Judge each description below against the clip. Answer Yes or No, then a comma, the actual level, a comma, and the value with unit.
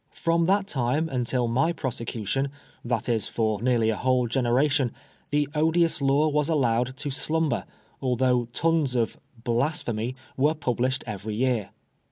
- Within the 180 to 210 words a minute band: No, average, 150 wpm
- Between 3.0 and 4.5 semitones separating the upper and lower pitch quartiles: Yes, average, 3.9 semitones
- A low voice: Yes, low, 130 Hz